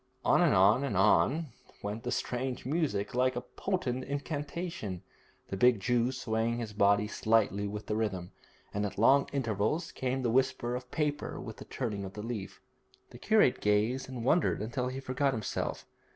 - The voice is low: Yes, low, 120 Hz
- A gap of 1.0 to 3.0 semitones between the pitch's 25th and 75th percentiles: No, average, 4.1 semitones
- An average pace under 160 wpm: No, average, 175 wpm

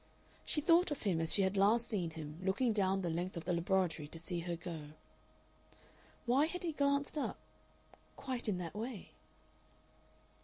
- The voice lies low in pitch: No, high, 190 Hz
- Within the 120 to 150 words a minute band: No, average, 175 wpm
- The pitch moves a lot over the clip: Yes, wide, 6.7 semitones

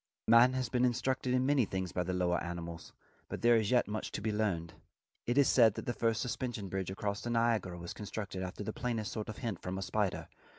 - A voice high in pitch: No, low, 110 Hz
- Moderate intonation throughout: Yes, average, 4.2 semitones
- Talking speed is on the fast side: Yes, fast, 225 wpm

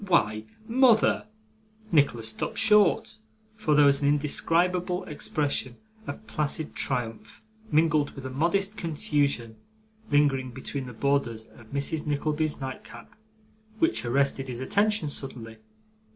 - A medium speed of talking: No, slow, 125 wpm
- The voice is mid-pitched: Yes, medium, 145 Hz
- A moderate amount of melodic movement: Yes, average, 4.7 semitones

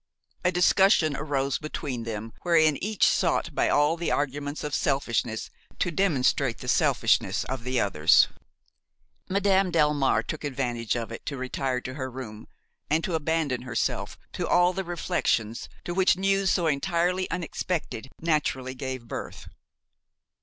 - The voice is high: No, medium, 145 Hz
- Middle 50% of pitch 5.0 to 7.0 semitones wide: Yes, average, 5.3 semitones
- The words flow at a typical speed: Yes, average, 145 wpm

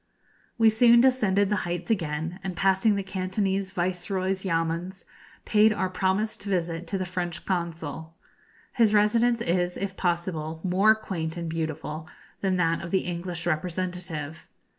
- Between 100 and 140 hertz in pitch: No, medium, 185 Hz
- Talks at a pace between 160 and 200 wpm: No, average, 140 wpm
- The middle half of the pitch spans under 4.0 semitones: Yes, average, 2.8 semitones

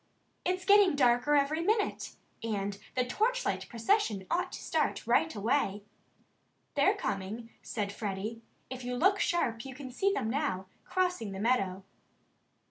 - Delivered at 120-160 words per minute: Yes, average, 140 wpm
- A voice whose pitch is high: Yes, very high, 250 Hz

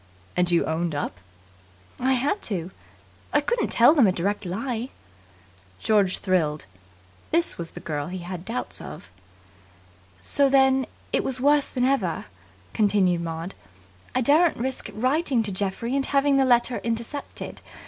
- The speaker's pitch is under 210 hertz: No, high, 230 Hz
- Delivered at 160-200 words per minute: No, average, 150 wpm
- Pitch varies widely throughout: Yes, wide, 6.9 semitones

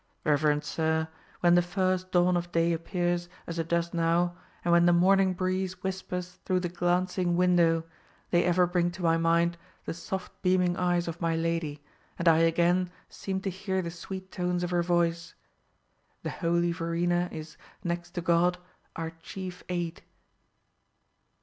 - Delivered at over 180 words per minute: No, average, 160 wpm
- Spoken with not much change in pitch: Yes, narrow, 1.3 semitones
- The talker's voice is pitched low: No, medium, 175 Hz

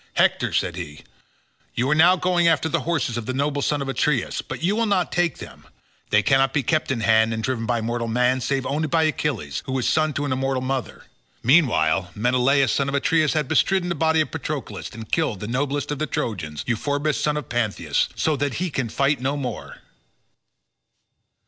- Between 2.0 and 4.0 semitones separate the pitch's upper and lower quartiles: No, average, 4.5 semitones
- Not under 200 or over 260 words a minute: Yes, fast, 205 wpm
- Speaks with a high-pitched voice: No, low, 135 Hz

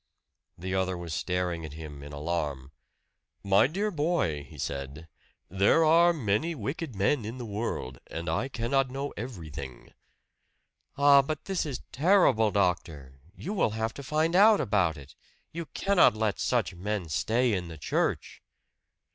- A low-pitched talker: Yes, low, 105 Hz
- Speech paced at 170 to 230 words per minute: No, average, 155 wpm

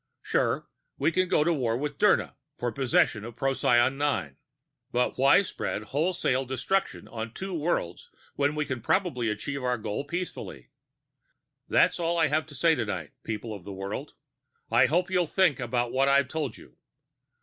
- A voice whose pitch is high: No, low, 135 Hz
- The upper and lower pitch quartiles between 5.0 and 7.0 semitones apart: Yes, average, 5.3 semitones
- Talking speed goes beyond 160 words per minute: Yes, average, 170 wpm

